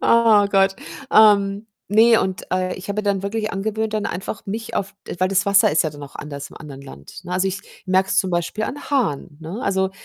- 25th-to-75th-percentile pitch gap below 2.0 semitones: No, average, 2.8 semitones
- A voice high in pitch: Yes, high, 195 Hz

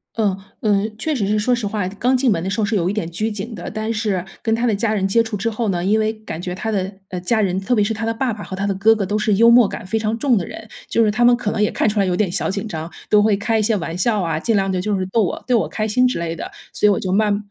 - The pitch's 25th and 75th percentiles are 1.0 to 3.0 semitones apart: Yes, narrow, 2.6 semitones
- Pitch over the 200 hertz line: Yes, high, 210 Hz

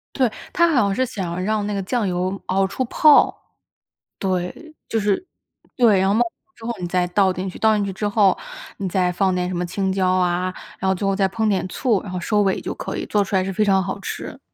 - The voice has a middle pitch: No, high, 195 Hz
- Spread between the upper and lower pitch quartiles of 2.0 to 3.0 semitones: Yes, narrow, 2.5 semitones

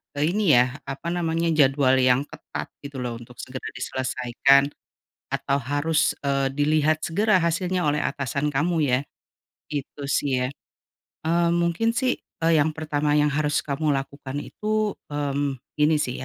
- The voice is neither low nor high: Yes, medium, 145 Hz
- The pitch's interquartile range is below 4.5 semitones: Yes, average, 3.2 semitones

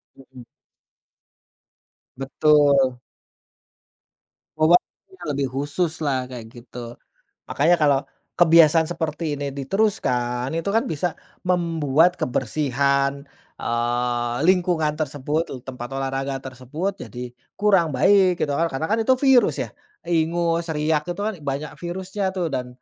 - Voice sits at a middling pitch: Yes, medium, 150 Hz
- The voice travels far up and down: No, average, 4.5 semitones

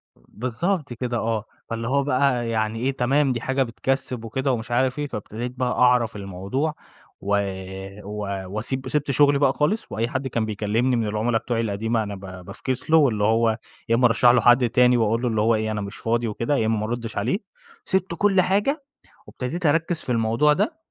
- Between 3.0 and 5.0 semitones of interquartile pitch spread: Yes, average, 3.4 semitones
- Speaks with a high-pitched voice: No, low, 120 Hz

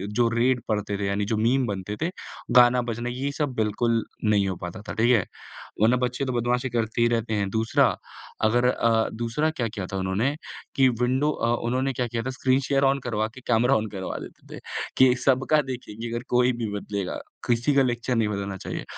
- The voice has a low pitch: Yes, low, 120 Hz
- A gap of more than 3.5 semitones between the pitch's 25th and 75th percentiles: No, average, 2.8 semitones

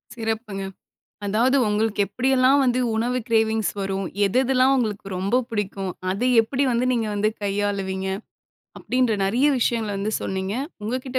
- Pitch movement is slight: No, average, 3.9 semitones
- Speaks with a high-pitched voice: Yes, high, 220 Hz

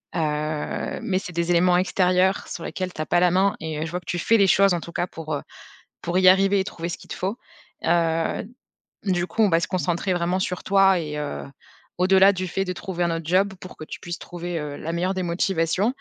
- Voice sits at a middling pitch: Yes, medium, 180 Hz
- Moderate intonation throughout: No, narrow, 2.2 semitones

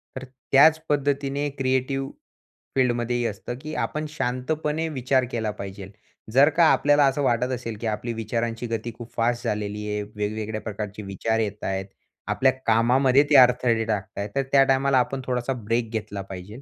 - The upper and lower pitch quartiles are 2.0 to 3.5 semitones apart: No, average, 3.9 semitones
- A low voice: Yes, low, 120 Hz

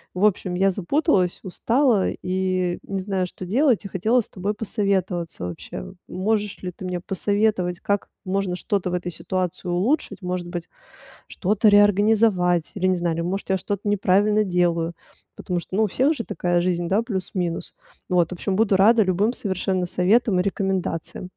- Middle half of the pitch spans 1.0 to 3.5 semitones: Yes, narrow, 2.5 semitones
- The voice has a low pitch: No, high, 190 Hz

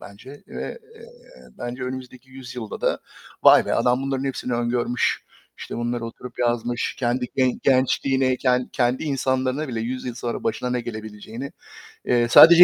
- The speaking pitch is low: Yes, low, 125 Hz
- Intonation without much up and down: Yes, narrow, 1.7 semitones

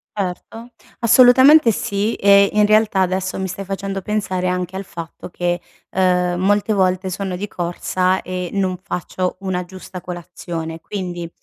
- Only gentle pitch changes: Yes, narrow, 2.0 semitones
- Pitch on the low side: No, high, 190 Hz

